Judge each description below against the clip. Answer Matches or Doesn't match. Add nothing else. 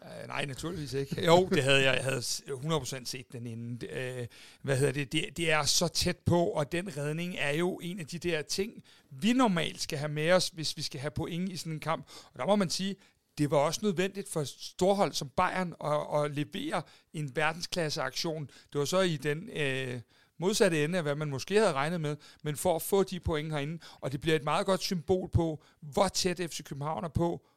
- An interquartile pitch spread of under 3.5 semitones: Doesn't match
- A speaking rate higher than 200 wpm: Matches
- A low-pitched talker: Doesn't match